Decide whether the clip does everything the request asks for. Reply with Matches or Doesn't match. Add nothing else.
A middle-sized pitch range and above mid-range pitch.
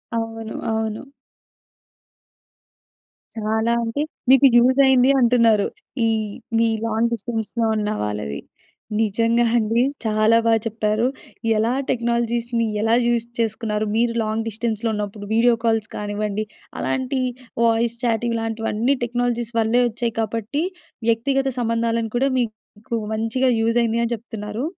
Doesn't match